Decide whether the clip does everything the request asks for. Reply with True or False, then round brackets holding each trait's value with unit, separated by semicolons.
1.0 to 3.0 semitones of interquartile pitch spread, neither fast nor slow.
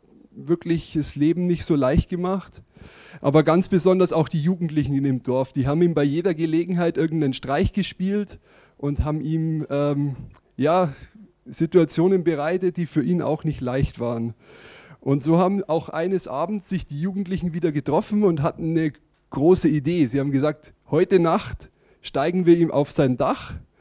False (3.6 semitones; 165 wpm)